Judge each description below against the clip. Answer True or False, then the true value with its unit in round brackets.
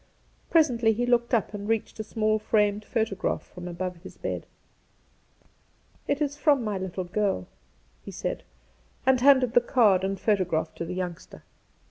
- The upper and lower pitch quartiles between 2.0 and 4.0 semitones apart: False (4.5 semitones)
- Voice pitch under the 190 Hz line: False (215 Hz)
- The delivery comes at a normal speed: True (160 wpm)